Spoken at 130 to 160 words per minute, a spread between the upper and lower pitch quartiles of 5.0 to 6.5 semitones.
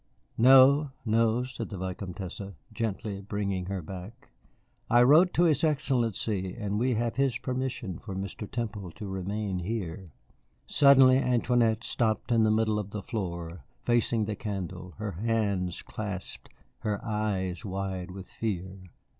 No: average, 140 wpm; average, 3.8 semitones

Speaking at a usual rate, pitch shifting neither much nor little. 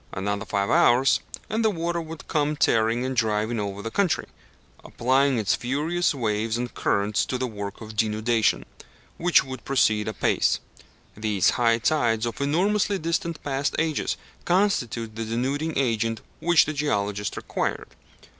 No: average, 145 wpm; wide, 6.0 semitones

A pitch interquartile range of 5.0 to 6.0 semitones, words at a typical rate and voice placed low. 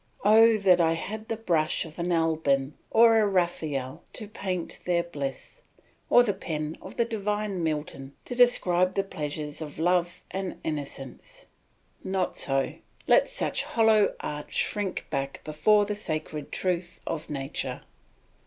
No: average, 5.3 semitones; average, 145 wpm; medium, 175 Hz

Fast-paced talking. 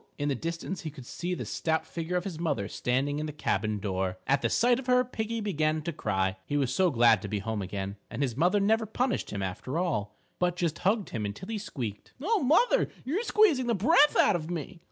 Yes: fast, 235 wpm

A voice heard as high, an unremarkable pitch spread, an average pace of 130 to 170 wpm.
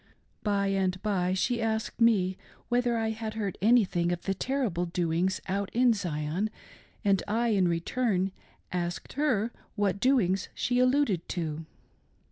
Yes: high, 200 Hz; average, 4.2 semitones; average, 140 wpm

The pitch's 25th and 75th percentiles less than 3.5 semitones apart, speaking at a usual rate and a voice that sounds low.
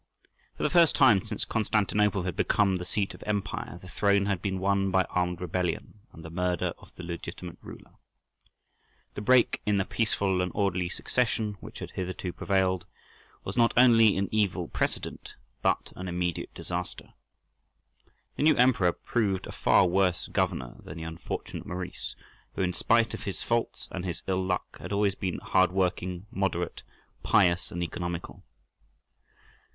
Yes: narrow, 2.5 semitones; average, 160 wpm; very low, 95 Hz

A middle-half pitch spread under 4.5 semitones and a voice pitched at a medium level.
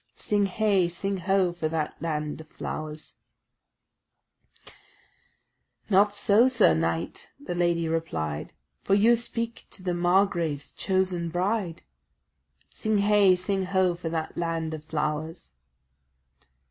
Yes: average, 3.7 semitones; medium, 175 Hz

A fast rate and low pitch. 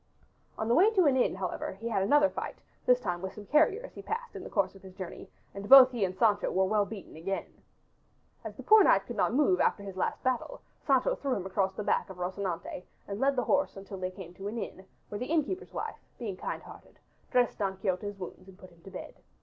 No: fast, 240 wpm; high, 205 Hz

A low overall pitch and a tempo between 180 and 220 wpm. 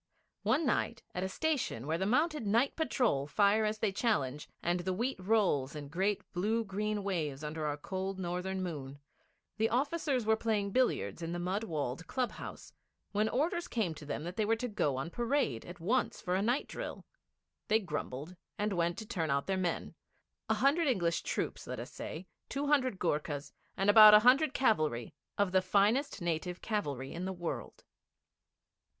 No: high, 195 Hz; average, 185 wpm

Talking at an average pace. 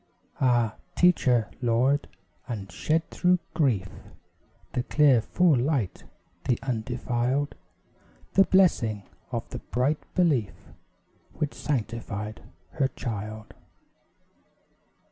No: slow, 95 wpm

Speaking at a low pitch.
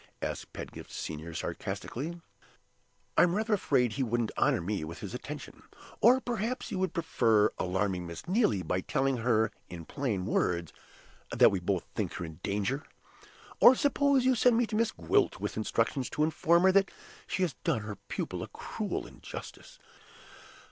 Yes: low, 125 Hz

